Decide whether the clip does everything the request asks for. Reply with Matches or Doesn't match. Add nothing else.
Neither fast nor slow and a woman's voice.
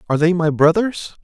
Doesn't match